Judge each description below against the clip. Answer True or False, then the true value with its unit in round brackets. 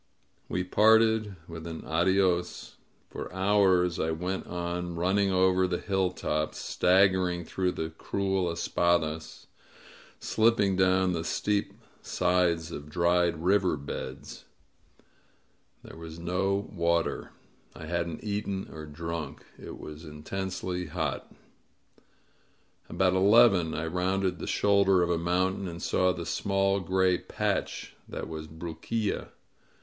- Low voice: True (90 Hz)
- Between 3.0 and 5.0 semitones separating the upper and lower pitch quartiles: False (2.4 semitones)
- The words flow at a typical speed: False (120 wpm)